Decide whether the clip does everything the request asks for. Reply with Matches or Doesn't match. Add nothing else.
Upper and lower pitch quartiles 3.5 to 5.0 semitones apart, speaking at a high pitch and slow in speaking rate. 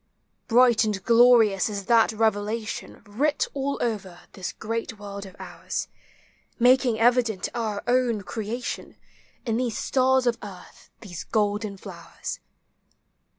Doesn't match